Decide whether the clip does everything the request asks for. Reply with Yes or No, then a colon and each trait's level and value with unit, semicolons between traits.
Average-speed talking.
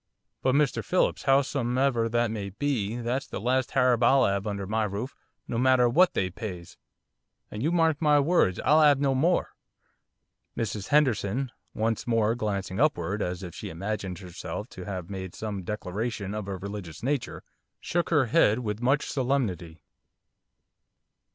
Yes: average, 160 wpm